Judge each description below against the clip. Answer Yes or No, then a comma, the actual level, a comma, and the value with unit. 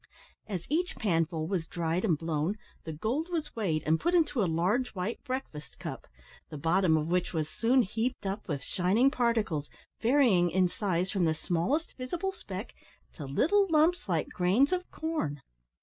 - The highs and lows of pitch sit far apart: Yes, wide, 8.0 semitones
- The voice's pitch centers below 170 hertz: No, high, 190 Hz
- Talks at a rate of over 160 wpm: Yes, average, 170 wpm